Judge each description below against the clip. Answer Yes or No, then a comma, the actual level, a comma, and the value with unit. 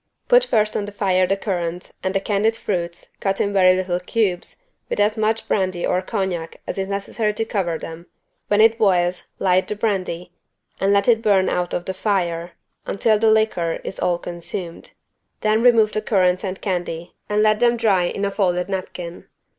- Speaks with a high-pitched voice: Yes, high, 195 Hz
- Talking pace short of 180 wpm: No, average, 190 wpm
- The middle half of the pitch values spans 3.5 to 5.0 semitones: No, average, 3.0 semitones